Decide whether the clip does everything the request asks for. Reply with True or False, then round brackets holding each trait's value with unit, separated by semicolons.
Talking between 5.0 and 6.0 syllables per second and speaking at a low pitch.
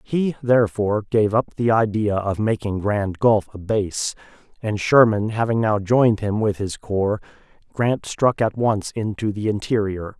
False (4.4 syllables/s; 105 Hz)